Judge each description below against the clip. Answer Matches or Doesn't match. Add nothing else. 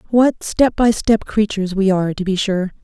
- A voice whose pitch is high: Matches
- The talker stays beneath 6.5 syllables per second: Matches